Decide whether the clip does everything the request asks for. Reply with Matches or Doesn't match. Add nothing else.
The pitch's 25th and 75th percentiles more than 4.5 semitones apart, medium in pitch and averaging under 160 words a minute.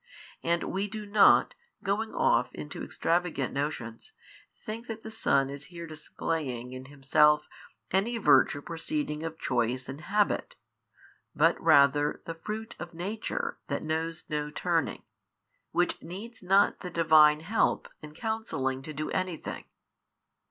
Matches